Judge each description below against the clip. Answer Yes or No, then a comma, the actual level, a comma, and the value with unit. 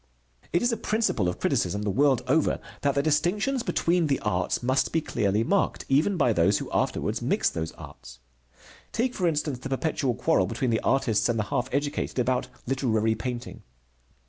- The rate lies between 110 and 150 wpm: No, average, 180 wpm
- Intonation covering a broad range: Yes, wide, 6.0 semitones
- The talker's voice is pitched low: Yes, low, 130 Hz